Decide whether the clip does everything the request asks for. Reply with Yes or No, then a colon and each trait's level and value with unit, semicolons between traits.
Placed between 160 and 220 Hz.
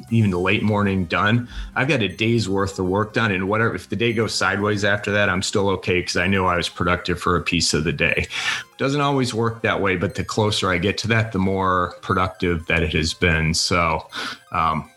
No: very low, 95 Hz